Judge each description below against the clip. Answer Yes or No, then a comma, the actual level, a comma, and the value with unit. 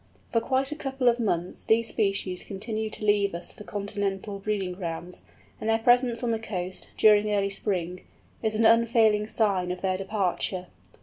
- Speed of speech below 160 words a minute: No, average, 175 wpm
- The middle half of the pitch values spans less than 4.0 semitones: Yes, average, 2.9 semitones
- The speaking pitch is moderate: No, high, 210 Hz